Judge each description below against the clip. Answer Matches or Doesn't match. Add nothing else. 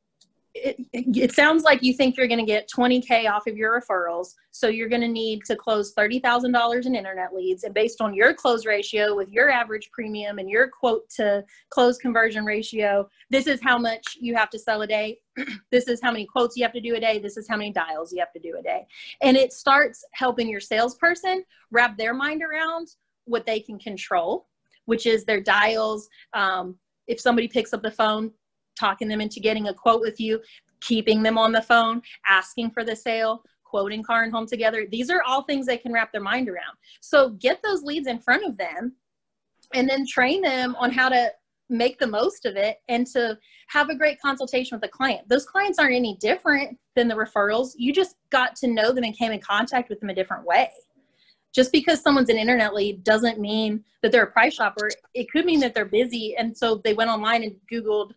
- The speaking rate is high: Matches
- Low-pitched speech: Doesn't match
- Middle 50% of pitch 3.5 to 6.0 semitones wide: Doesn't match